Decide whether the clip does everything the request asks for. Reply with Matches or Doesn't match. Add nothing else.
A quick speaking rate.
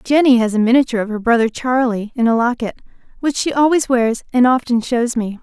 Matches